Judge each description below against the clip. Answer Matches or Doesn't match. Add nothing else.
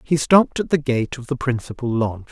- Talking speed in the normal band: Doesn't match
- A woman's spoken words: Doesn't match